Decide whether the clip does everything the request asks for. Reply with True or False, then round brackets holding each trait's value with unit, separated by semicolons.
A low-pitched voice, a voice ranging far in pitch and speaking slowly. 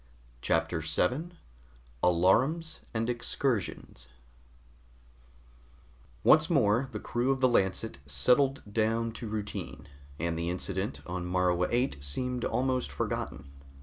True (110 Hz; 6.2 semitones; 110 wpm)